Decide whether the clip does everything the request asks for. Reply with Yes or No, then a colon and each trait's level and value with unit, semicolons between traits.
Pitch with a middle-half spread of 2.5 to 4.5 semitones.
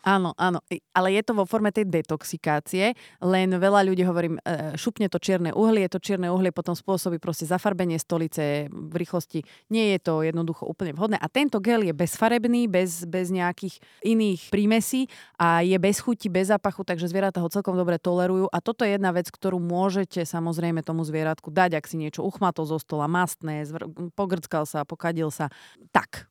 Yes: average, 2.8 semitones